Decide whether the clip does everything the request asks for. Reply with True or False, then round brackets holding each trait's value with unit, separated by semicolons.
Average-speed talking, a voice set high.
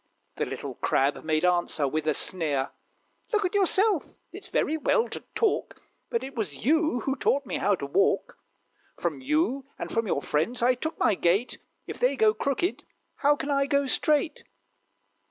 True (175 wpm; 270 Hz)